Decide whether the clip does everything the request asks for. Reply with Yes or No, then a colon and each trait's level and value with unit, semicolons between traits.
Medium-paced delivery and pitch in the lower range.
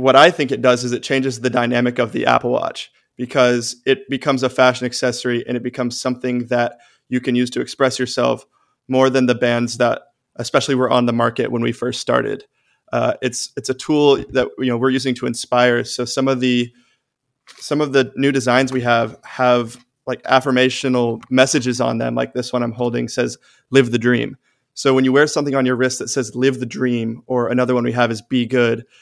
No: fast, 215 wpm; low, 125 Hz